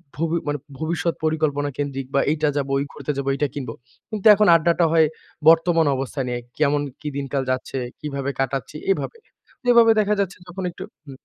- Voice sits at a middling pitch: Yes, medium, 150 Hz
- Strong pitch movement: No, average, 3.4 semitones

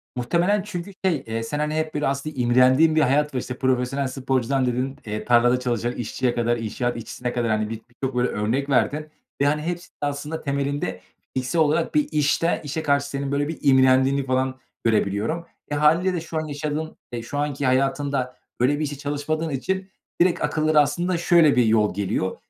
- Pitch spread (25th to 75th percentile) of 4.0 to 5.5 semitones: No, average, 3.6 semitones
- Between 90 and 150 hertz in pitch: Yes, medium, 140 Hz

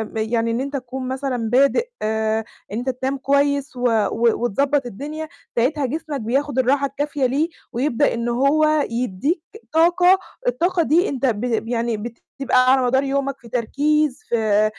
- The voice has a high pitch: Yes, very high, 265 Hz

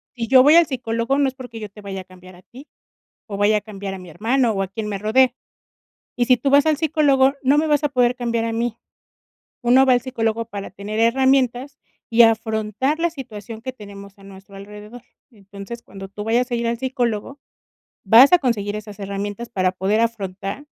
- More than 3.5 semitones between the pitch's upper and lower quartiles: Yes, average, 4.3 semitones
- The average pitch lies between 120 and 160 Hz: No, high, 230 Hz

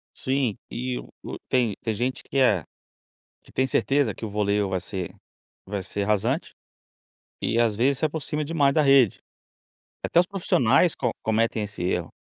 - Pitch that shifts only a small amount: No, average, 5.0 semitones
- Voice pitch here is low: Yes, low, 120 Hz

